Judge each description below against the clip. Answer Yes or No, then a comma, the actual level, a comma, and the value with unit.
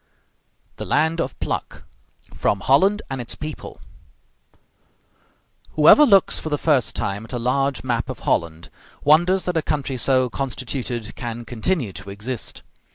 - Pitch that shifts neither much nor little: Yes, average, 4.7 semitones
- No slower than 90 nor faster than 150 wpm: Yes, average, 145 wpm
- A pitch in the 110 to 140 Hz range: Yes, low, 135 Hz